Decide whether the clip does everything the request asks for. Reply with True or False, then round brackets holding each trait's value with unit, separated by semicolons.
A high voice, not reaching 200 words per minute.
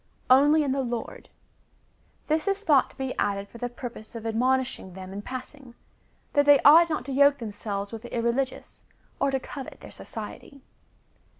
True (260 Hz; 175 wpm)